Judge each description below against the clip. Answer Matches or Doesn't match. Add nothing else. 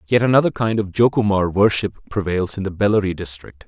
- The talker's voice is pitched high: Doesn't match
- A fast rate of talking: Doesn't match